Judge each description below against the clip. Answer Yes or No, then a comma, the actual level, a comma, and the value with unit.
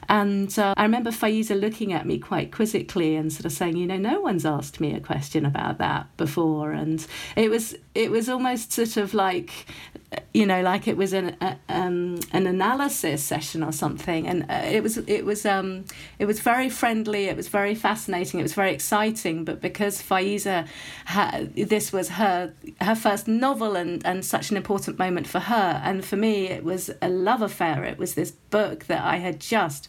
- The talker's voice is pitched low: No, high, 190 Hz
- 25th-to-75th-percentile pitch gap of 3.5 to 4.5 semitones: Yes, average, 3.8 semitones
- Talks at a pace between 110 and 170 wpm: No, average, 200 wpm